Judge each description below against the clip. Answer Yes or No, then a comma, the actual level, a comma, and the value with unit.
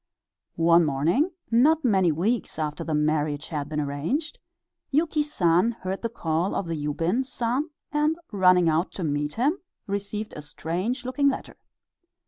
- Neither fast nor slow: Yes, average, 150 wpm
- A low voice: No, medium, 185 Hz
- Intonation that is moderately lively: No, wide, 8.1 semitones